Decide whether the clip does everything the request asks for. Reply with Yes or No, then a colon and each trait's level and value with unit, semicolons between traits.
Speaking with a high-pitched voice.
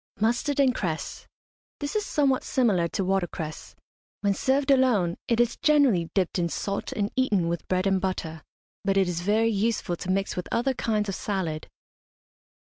Yes: high, 200 Hz